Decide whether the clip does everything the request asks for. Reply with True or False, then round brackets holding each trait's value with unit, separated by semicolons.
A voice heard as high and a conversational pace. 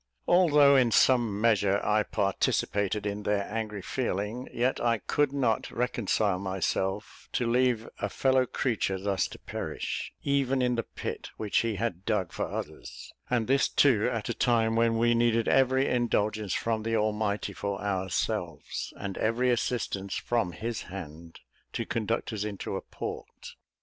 False (110 Hz; 155 wpm)